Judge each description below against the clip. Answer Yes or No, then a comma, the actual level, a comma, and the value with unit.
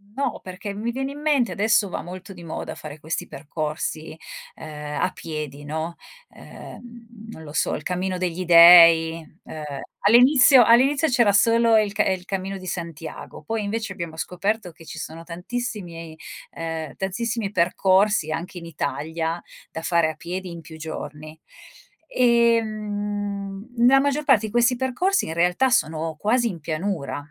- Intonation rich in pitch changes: Yes, wide, 5.8 semitones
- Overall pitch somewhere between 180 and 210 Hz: Yes, medium, 185 Hz